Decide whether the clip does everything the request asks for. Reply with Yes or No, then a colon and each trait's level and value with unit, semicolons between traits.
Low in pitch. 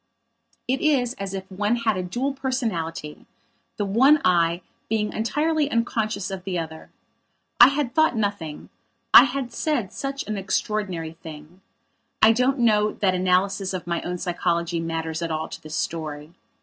No: high, 195 Hz